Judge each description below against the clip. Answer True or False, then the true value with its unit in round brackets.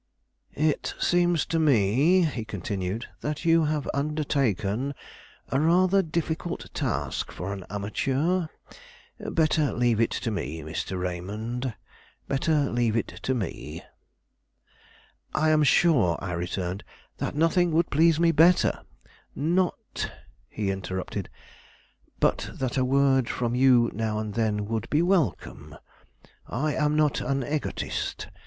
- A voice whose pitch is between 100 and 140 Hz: True (135 Hz)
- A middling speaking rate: False (130 wpm)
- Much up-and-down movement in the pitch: True (6.9 semitones)